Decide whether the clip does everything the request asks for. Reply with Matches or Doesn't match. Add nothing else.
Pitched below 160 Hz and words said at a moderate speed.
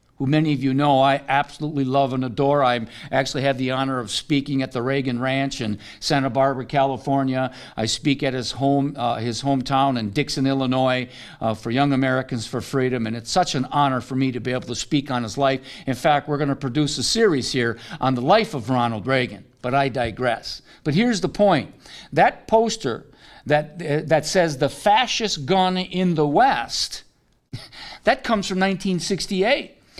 Matches